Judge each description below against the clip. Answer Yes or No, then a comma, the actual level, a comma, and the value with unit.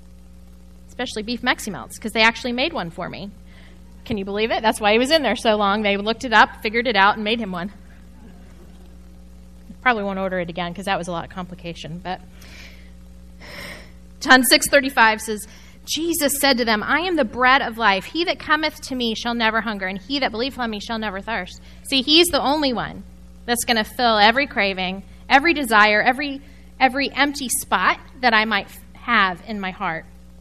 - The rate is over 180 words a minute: Yes, average, 200 wpm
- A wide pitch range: Yes, wide, 6.7 semitones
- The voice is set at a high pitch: Yes, high, 215 Hz